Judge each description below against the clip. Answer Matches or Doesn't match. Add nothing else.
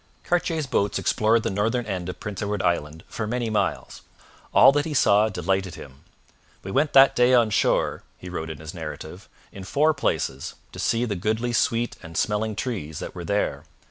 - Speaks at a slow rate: Doesn't match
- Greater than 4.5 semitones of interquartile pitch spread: Matches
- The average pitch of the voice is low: Matches